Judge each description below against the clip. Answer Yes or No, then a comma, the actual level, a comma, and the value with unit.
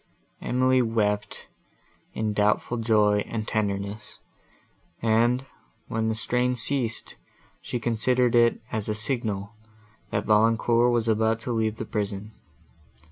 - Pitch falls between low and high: No, low, 110 Hz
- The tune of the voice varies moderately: No, narrow, 2.0 semitones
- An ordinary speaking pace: No, slow, 120 wpm